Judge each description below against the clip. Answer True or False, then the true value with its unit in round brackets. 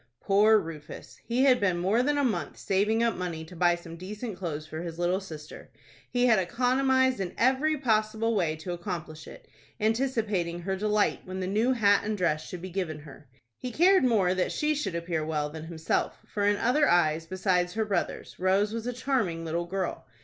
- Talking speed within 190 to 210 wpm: True (200 wpm)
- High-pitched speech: True (195 Hz)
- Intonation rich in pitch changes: False (5.0 semitones)